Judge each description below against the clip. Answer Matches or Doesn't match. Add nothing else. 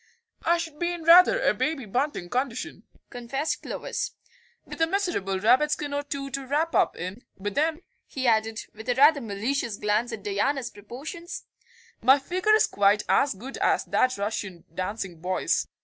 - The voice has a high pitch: Matches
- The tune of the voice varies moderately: Doesn't match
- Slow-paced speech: Doesn't match